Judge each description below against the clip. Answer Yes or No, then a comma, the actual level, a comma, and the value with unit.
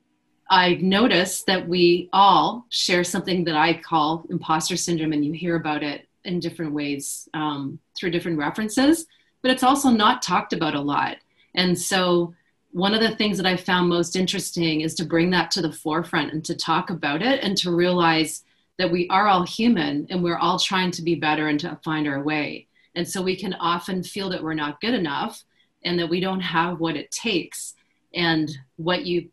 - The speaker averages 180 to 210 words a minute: Yes, average, 200 wpm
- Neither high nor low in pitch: Yes, medium, 175 Hz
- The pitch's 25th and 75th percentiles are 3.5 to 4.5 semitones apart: No, narrow, 2.6 semitones